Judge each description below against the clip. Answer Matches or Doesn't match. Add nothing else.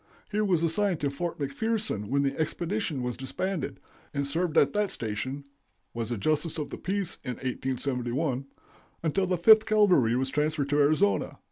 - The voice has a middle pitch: Matches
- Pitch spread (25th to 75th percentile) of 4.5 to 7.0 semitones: Matches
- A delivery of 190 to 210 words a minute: Doesn't match